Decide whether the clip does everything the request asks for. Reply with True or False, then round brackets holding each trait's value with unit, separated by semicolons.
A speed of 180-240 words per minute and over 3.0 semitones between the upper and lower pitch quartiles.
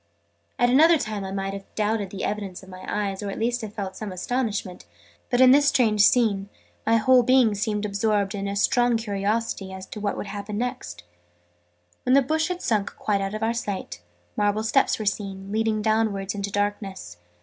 False (195 wpm; 2.5 semitones)